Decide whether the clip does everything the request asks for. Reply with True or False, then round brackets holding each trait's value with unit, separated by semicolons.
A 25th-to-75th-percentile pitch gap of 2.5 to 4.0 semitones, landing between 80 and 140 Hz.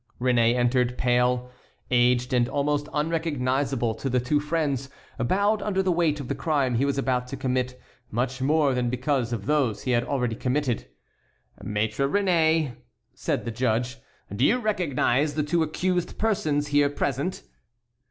True (3.6 semitones; 135 Hz)